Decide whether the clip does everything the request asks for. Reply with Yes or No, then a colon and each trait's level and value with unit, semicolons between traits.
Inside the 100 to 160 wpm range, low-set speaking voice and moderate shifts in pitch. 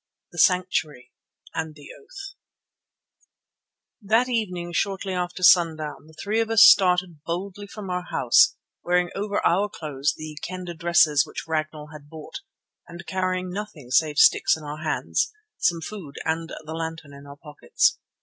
No: average, 150 wpm; medium, 175 Hz; average, 3.6 semitones